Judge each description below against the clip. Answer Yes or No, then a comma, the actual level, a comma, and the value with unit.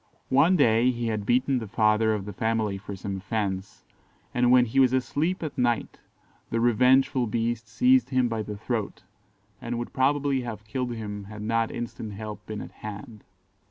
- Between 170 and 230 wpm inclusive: Yes, average, 180 wpm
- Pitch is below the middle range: Yes, low, 115 Hz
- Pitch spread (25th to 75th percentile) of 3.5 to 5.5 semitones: No, average, 2.9 semitones